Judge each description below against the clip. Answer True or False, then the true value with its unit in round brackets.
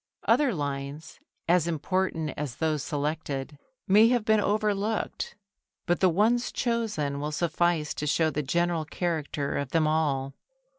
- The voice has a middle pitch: True (160 Hz)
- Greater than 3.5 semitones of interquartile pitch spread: True (4.3 semitones)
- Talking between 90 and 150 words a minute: True (140 wpm)